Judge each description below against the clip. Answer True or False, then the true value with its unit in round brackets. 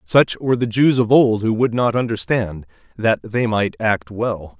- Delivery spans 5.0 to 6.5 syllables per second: False (4.3 syllables/s)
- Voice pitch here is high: False (110 Hz)